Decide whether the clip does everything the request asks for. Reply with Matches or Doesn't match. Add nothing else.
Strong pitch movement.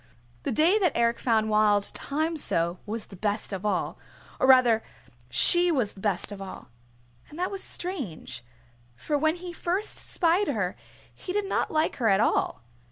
Matches